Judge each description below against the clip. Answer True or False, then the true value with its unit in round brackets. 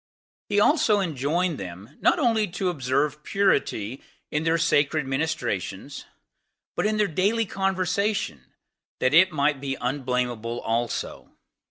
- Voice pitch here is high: False (150 Hz)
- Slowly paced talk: True (125 wpm)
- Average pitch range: False (6.9 semitones)